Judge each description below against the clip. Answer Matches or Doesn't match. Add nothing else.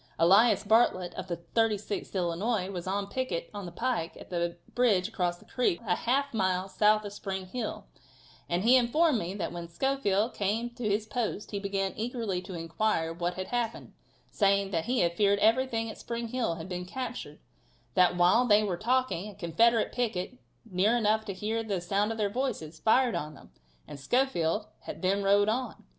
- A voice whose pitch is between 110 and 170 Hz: Doesn't match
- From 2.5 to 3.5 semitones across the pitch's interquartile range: Doesn't match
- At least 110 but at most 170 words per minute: Doesn't match